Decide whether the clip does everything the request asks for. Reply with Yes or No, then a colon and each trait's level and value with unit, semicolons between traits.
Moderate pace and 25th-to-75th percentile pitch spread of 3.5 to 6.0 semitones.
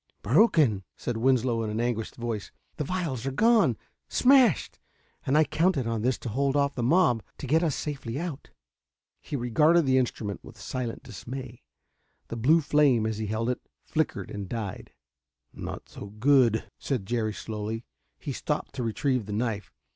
Yes: average, 170 wpm; average, 4.3 semitones